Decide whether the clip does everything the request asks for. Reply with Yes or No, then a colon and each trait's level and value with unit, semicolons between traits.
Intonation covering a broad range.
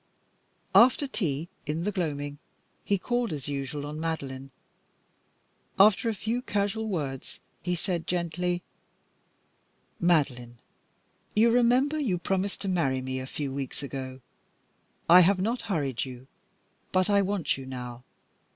Yes: wide, 6.7 semitones